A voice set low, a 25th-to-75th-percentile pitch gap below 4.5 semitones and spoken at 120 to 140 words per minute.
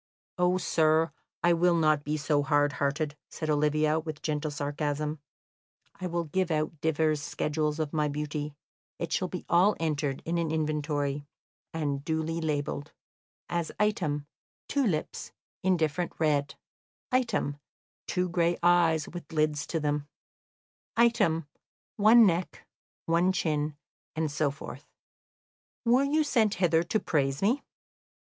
No: medium, 155 Hz; average, 2.7 semitones; slow, 135 wpm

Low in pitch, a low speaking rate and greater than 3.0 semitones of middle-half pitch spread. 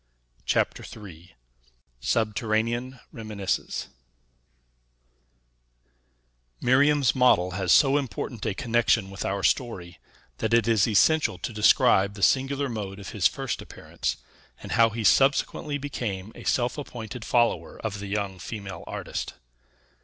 Yes: low, 110 Hz; slow, 125 wpm; average, 4.1 semitones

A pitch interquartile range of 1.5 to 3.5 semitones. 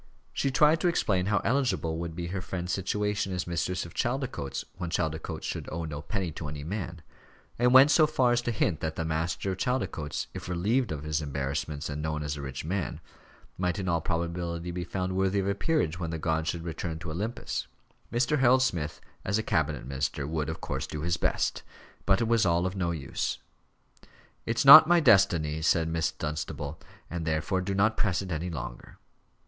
No: average, 4.4 semitones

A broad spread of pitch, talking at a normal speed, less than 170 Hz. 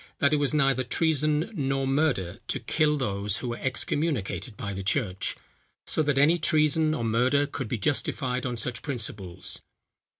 No: average, 4.6 semitones; average, 165 wpm; low, 135 Hz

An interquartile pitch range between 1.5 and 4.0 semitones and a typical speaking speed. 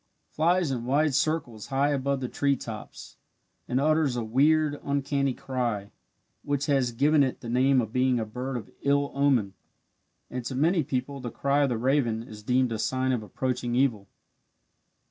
Yes: average, 2.7 semitones; average, 175 wpm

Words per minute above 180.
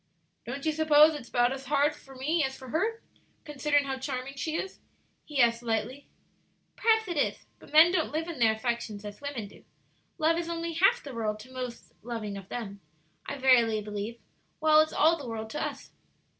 Yes: average, 200 wpm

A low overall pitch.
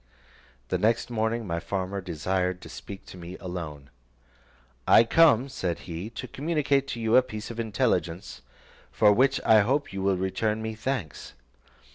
Yes: low, 105 Hz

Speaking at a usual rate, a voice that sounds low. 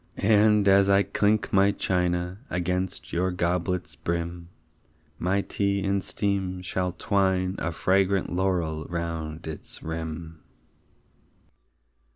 No: slow, 110 wpm; very low, 90 Hz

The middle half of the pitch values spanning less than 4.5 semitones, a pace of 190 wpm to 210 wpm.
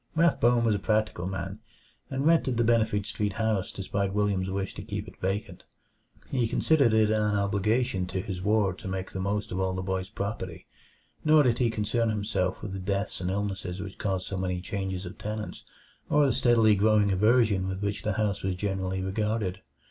Yes: narrow, 2.6 semitones; average, 195 wpm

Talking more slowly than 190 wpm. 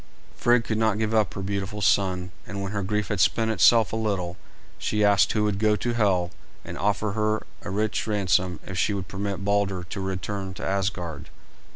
No: average, 200 wpm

